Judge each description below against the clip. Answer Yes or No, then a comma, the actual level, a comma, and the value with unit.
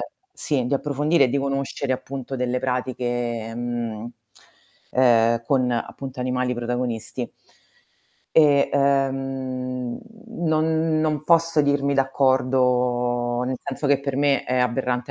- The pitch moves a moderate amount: No, narrow, 2.2 semitones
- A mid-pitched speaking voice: No, low, 130 Hz